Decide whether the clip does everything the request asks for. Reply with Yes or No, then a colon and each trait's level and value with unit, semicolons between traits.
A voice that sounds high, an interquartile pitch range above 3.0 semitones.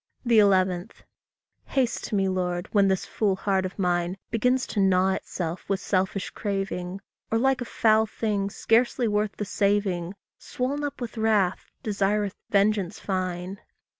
No: high, 200 Hz; average, 2.7 semitones